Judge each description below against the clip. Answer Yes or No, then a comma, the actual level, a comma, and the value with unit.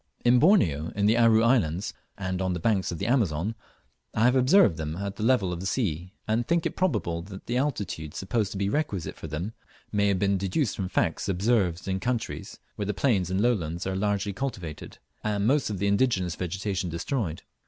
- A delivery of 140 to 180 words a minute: No, fast, 205 wpm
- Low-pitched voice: Yes, low, 100 Hz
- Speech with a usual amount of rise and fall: Yes, average, 4.4 semitones